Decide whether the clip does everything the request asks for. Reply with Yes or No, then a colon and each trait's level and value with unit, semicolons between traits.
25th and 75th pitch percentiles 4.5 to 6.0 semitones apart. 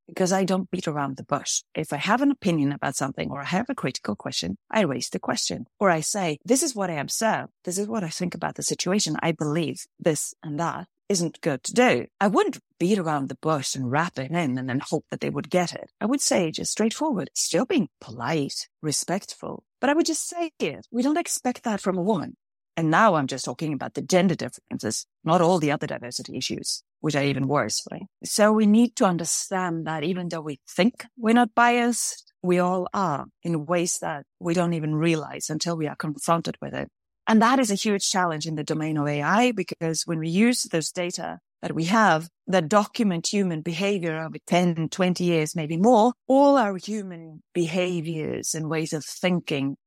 Yes: average, 5.1 semitones